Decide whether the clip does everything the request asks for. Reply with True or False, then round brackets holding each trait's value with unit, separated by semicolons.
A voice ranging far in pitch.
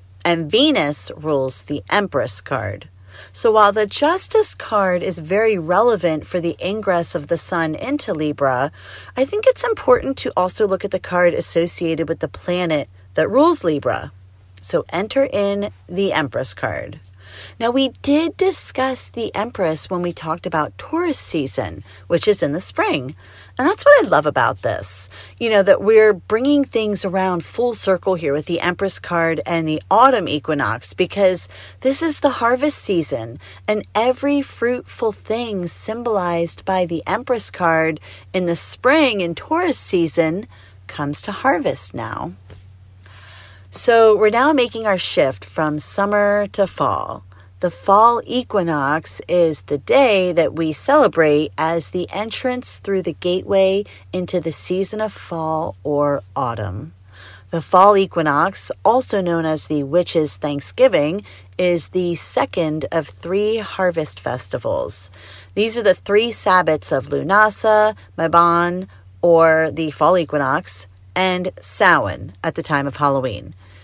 True (6.4 semitones)